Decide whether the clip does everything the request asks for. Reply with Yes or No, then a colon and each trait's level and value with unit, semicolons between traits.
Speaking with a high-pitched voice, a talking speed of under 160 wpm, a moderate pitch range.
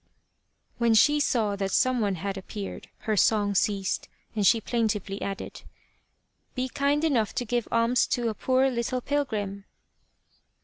Yes: high, 225 Hz; average, 150 wpm; average, 3.9 semitones